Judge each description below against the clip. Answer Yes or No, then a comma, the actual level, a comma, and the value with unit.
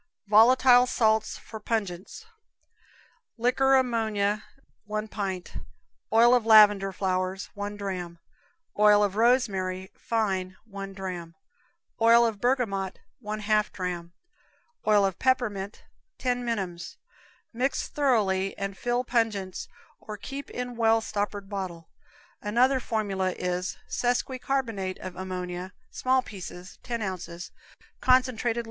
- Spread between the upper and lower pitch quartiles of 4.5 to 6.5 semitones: No, average, 3.9 semitones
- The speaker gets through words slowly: Yes, slow, 105 wpm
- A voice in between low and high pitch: No, high, 210 Hz